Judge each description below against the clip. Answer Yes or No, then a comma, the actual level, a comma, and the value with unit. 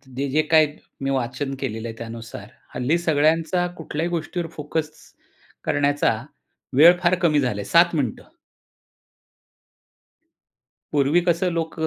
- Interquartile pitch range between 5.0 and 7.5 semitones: No, average, 4.1 semitones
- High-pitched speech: No, medium, 150 Hz